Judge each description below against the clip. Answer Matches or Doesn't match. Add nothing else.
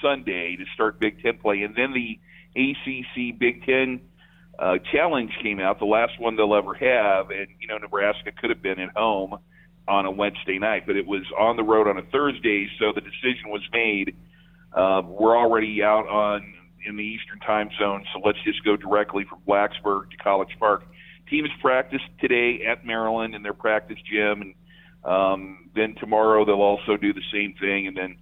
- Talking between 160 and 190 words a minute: Matches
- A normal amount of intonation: Matches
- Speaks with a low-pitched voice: Matches